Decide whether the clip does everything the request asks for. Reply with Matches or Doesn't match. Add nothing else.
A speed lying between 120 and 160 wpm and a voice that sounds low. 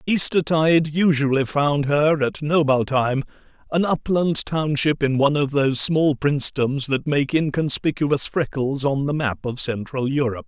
Doesn't match